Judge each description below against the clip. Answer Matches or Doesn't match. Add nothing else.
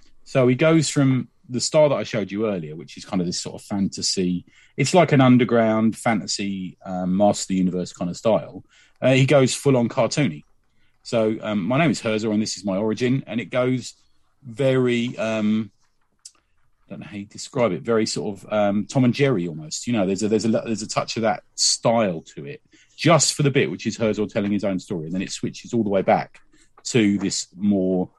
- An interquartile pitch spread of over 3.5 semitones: Matches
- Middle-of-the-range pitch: Doesn't match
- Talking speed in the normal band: Doesn't match